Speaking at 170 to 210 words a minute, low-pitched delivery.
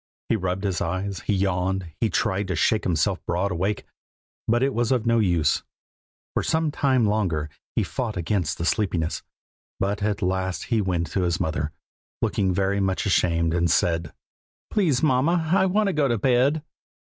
Yes: average, 175 wpm; low, 100 Hz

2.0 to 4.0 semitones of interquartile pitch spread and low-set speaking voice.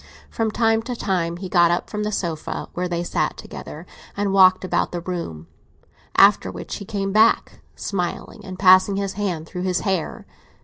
No: average, 2.8 semitones; medium, 185 Hz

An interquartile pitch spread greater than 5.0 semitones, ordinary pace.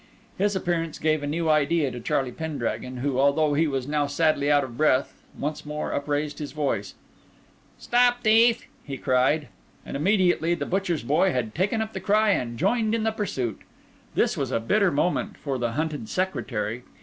Yes: wide, 5.5 semitones; average, 180 wpm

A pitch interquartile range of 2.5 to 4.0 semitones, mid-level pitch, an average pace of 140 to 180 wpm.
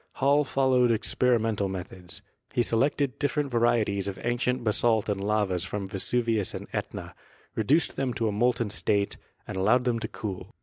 No: average, 3.7 semitones; low, 115 Hz; average, 165 wpm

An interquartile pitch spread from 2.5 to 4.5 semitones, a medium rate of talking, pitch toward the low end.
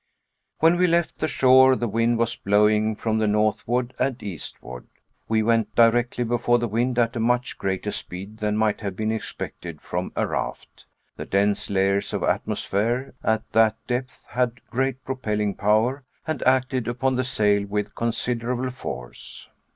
Yes: average, 3.1 semitones; average, 160 wpm; low, 115 Hz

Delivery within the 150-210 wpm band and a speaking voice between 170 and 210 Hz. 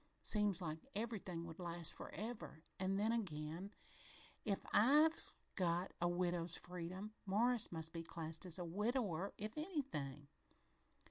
No: slow, 135 wpm; medium, 185 Hz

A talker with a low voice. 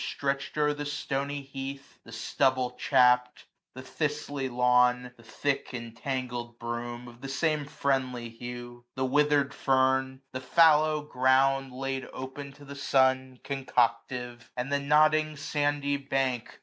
Yes: low, 130 Hz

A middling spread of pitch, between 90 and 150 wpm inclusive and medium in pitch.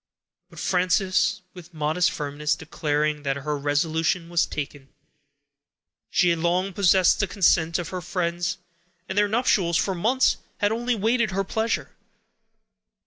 Yes: average, 3.8 semitones; average, 140 wpm; medium, 175 Hz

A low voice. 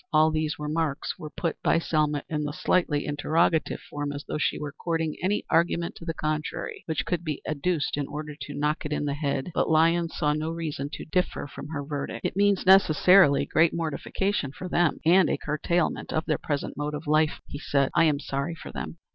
No: medium, 155 Hz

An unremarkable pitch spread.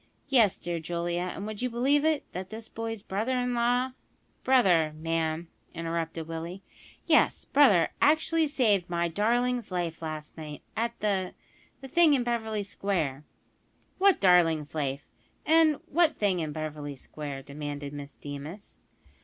No: wide, 7.1 semitones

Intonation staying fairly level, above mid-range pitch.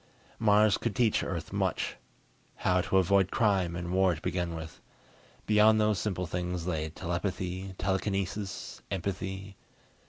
No: narrow, 2.2 semitones; very low, 95 Hz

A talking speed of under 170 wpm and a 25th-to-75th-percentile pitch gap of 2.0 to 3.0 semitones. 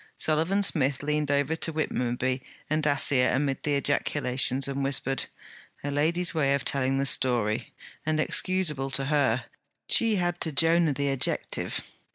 Yes: average, 150 wpm; narrow, 2.6 semitones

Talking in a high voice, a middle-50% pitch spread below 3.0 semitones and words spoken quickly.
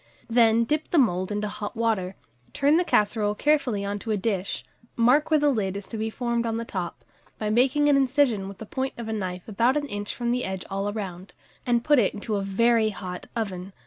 No: high, 220 Hz; average, 3.7 semitones; fast, 225 wpm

